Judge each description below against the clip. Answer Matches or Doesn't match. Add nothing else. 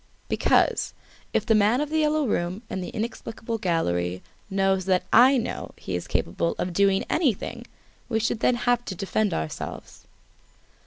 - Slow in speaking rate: Doesn't match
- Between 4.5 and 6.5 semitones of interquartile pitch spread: Matches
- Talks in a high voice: Matches